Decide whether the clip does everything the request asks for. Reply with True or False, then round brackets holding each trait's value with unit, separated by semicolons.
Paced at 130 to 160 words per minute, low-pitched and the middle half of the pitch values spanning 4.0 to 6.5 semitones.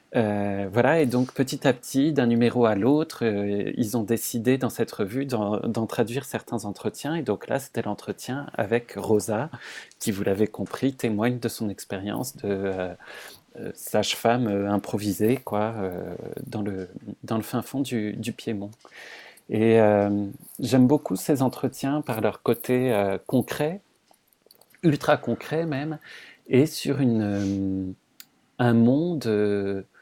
True (150 wpm; 115 Hz; 4.3 semitones)